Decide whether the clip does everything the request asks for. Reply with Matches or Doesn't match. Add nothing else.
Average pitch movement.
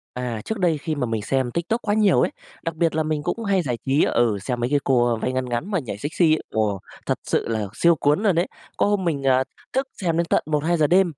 Doesn't match